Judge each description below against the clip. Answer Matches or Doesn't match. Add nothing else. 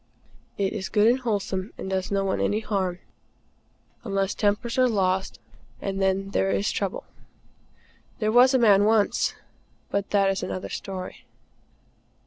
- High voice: Matches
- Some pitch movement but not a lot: Doesn't match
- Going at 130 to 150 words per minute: Matches